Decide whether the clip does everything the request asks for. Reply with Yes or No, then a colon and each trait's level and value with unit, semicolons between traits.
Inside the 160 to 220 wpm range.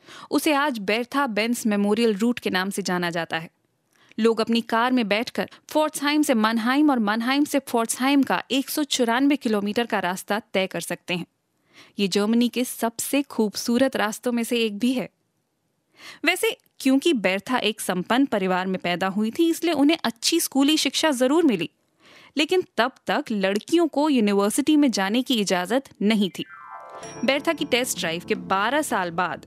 Yes: average, 165 wpm